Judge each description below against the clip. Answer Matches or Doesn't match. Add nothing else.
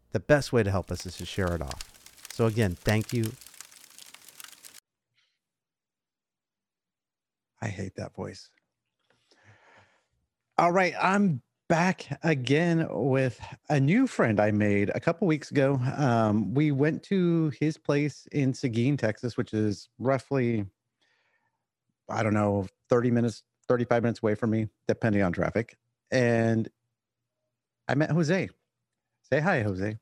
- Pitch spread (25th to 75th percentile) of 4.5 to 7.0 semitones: Matches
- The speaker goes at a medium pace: Doesn't match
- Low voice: Matches